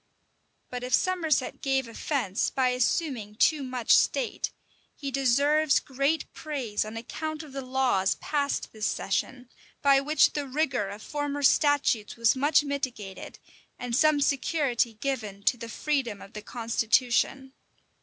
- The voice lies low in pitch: No, very high, 265 Hz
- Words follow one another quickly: No, average, 145 wpm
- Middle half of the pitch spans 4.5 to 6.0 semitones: No, average, 3.8 semitones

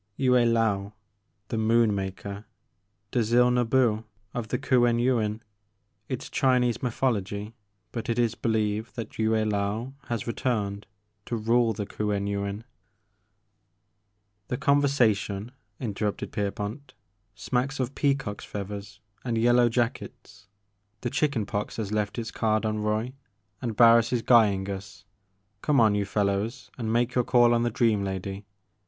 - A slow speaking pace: No, average, 145 wpm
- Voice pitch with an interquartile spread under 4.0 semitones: Yes, average, 2.9 semitones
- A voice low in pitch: Yes, low, 110 Hz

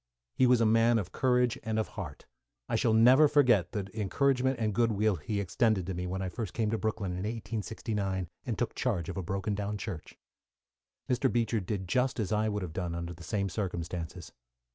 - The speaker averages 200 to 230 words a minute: Yes, fast, 205 wpm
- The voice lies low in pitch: Yes, low, 105 Hz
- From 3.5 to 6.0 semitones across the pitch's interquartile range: Yes, average, 3.8 semitones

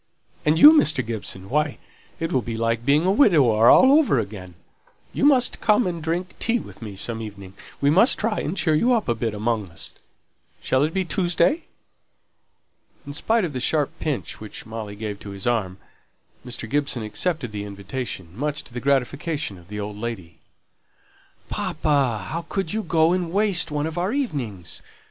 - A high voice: No, medium, 140 Hz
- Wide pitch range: Yes, wide, 8.1 semitones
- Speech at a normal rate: Yes, average, 175 wpm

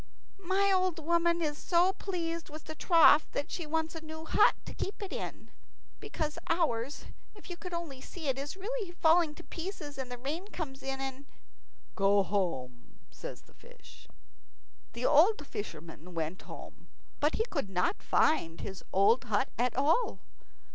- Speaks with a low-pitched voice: No, very high, 310 Hz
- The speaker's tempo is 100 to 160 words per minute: No, average, 170 wpm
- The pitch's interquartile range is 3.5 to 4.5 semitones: No, wide, 5.6 semitones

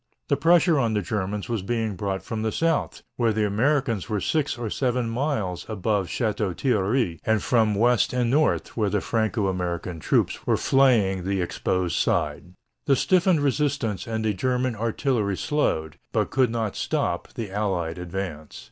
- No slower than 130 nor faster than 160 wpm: No, average, 170 wpm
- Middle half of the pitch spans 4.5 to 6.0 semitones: Yes, average, 4.8 semitones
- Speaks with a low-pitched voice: Yes, low, 110 Hz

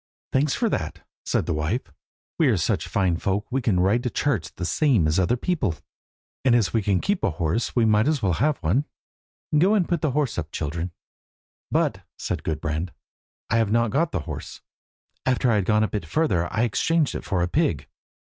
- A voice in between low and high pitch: No, low, 110 Hz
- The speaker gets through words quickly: Yes, fast, 210 wpm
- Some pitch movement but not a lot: No, wide, 7.6 semitones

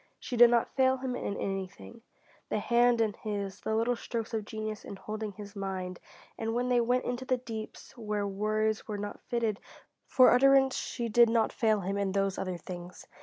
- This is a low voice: No, high, 220 Hz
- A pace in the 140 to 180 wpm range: No, average, 195 wpm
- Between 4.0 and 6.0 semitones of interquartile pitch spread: No, average, 3.1 semitones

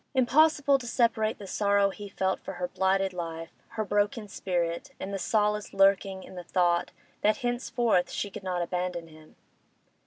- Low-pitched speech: No, high, 195 Hz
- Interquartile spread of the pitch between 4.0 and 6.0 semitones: No, average, 3.3 semitones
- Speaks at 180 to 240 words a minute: No, average, 165 wpm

